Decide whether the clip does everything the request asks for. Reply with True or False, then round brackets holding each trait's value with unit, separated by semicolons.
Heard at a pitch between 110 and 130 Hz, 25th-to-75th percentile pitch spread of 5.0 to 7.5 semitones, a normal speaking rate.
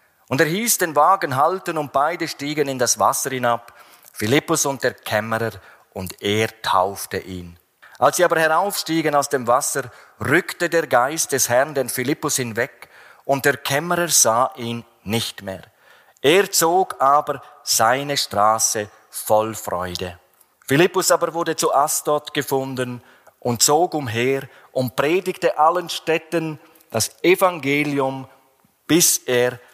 False (140 Hz; 5.3 semitones; 135 wpm)